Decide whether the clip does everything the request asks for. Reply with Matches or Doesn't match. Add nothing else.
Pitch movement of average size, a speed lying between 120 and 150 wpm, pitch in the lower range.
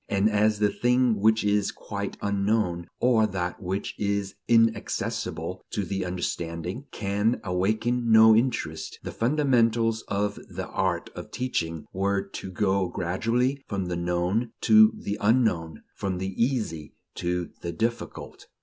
Matches